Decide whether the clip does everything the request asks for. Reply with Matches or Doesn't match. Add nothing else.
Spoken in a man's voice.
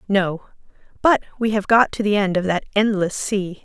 Doesn't match